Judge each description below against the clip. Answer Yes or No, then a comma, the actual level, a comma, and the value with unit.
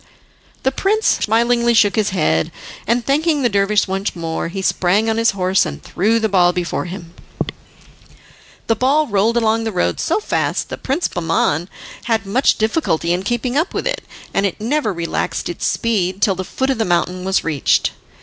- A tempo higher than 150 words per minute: Yes, average, 185 wpm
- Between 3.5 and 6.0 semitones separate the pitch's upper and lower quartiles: Yes, average, 4.6 semitones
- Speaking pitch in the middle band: No, high, 210 Hz